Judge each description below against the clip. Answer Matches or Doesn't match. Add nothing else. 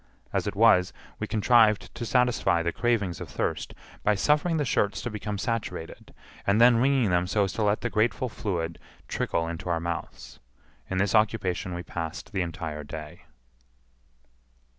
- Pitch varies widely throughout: Doesn't match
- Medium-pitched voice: Doesn't match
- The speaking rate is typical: Matches